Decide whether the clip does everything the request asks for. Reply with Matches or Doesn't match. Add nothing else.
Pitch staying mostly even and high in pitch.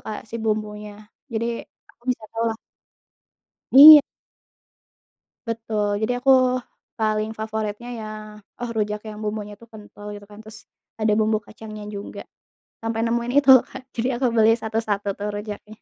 Matches